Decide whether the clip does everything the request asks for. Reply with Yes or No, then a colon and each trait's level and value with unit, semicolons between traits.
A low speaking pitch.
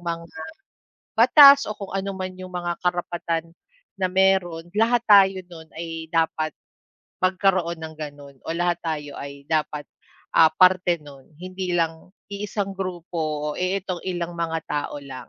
No: medium, 175 Hz